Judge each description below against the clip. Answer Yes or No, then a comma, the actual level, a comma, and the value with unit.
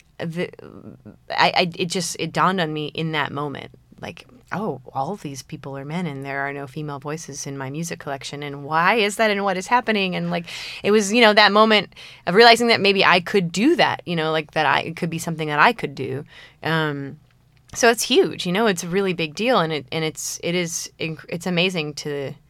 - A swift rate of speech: Yes, fast, 230 wpm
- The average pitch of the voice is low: No, medium, 165 Hz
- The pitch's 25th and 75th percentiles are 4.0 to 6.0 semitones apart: Yes, average, 4.9 semitones